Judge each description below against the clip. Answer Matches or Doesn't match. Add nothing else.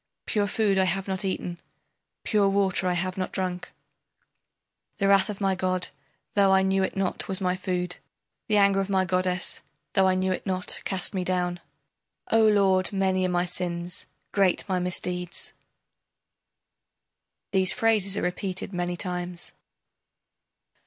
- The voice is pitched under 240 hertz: Matches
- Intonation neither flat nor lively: Doesn't match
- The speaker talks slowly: Doesn't match